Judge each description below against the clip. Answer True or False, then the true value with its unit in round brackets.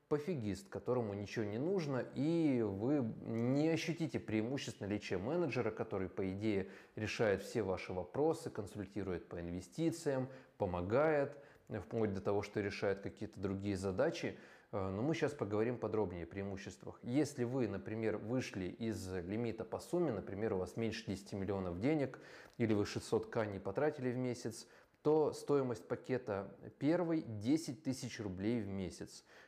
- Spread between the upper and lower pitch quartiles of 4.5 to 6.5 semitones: True (5.1 semitones)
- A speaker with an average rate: True (145 wpm)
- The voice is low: True (110 Hz)